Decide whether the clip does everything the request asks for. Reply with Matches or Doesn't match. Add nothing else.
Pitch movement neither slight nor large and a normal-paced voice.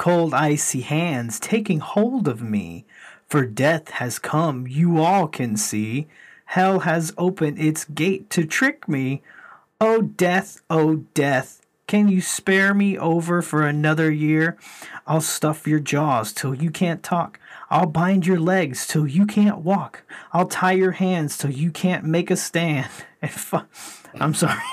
Matches